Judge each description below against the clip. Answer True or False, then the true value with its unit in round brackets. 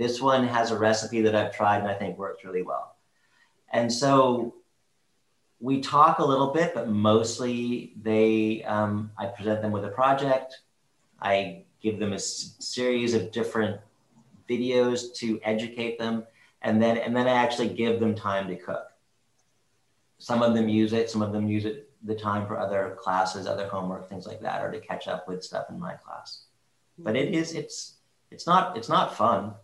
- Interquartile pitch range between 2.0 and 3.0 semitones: True (2.5 semitones)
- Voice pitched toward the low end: True (110 Hz)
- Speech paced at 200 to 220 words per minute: False (185 wpm)